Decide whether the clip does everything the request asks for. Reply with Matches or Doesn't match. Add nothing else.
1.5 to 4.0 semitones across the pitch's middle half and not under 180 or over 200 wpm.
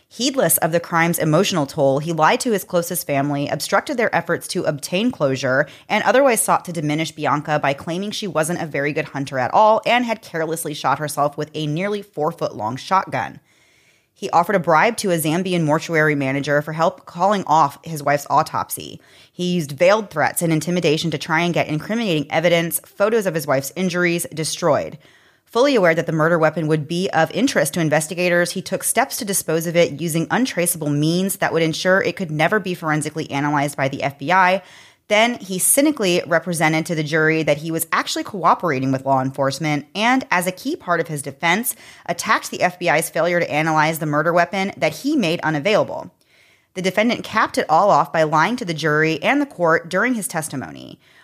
Matches